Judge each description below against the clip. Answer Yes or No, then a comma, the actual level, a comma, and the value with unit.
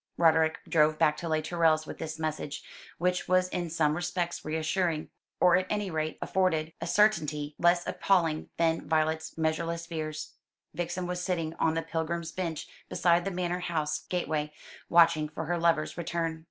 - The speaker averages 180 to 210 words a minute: No, average, 165 wpm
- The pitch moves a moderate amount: No, narrow, 2.0 semitones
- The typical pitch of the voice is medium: Yes, medium, 165 Hz